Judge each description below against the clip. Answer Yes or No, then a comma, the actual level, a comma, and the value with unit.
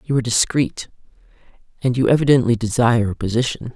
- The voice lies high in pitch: No, low, 120 Hz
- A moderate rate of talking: Yes, average, 145 wpm